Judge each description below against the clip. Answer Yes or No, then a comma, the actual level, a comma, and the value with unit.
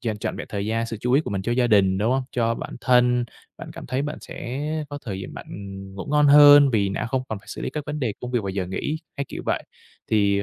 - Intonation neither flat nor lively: Yes, average, 4.8 semitones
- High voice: No, low, 120 Hz